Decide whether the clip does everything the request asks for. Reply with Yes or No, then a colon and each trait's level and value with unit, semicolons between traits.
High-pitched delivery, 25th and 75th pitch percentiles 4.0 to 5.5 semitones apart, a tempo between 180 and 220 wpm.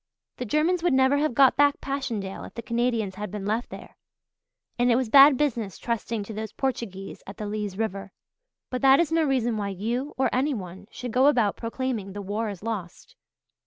Yes: high, 235 Hz; average, 4.5 semitones; average, 200 wpm